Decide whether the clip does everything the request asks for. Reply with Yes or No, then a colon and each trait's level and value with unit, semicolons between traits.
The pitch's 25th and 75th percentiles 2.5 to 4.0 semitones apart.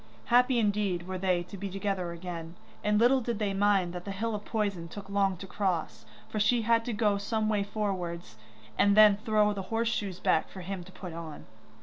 Yes: average, 2.8 semitones